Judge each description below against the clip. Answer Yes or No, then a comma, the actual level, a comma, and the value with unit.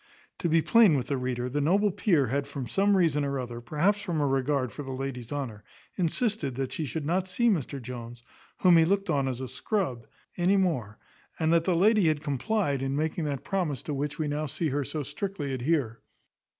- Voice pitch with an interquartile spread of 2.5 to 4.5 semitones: No, average, 4.9 semitones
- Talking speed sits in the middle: No, fast, 210 wpm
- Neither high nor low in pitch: Yes, medium, 145 Hz